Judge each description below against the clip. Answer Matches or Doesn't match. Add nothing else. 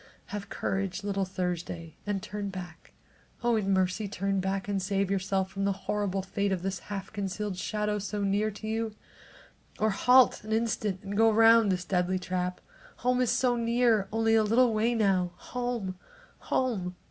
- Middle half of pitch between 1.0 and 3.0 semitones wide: Matches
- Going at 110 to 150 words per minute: Doesn't match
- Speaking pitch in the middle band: Doesn't match